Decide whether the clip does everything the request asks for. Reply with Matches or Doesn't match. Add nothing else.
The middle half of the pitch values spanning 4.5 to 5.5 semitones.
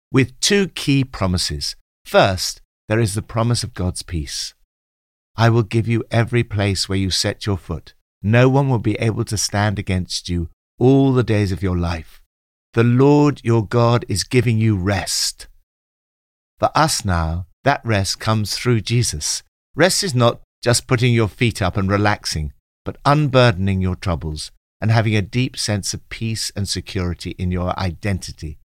Matches